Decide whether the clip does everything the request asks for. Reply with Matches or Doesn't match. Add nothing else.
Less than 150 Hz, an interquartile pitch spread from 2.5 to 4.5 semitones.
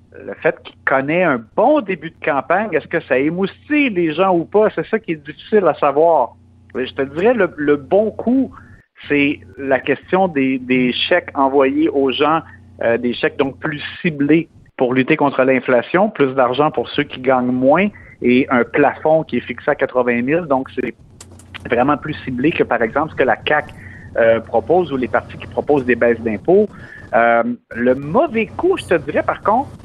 Doesn't match